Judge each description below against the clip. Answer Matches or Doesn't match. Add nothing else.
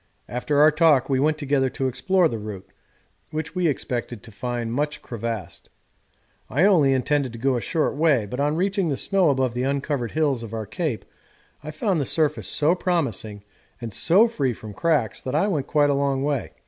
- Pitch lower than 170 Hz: Matches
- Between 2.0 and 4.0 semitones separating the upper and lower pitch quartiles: Doesn't match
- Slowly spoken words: Doesn't match